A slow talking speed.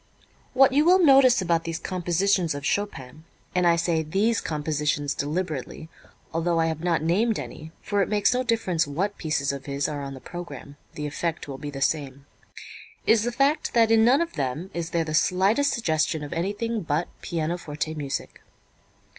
No: average, 180 wpm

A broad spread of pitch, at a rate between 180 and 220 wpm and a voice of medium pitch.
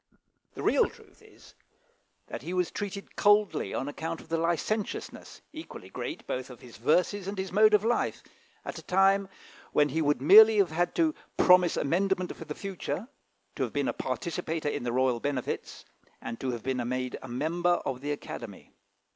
Yes: wide, 6.8 semitones; average, 185 wpm; medium, 165 Hz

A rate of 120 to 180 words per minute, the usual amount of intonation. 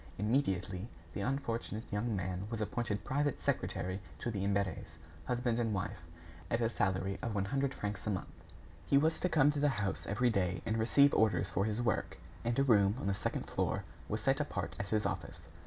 No: average, 200 wpm; average, 3.8 semitones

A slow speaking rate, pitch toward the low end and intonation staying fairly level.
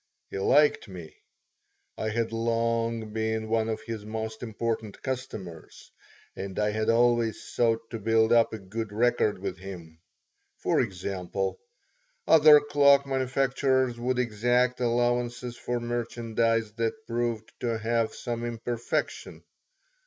Yes: slow, 125 wpm; low, 115 Hz; narrow, 1.8 semitones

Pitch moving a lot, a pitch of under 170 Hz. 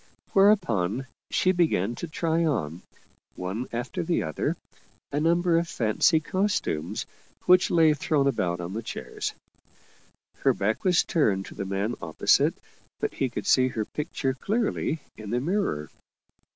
Yes: wide, 8.7 semitones; low, 135 Hz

